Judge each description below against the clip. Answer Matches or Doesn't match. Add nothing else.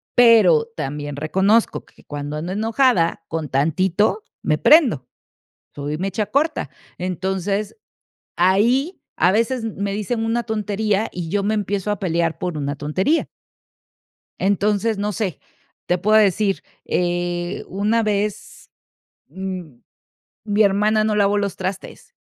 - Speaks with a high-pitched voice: Matches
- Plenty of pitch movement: Doesn't match